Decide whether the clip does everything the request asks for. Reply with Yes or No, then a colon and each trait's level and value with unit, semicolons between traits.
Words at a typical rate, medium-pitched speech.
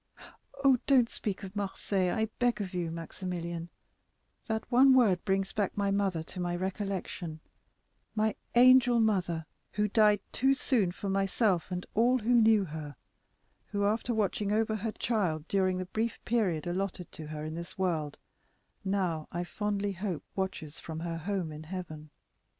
No: average, 155 wpm; high, 195 Hz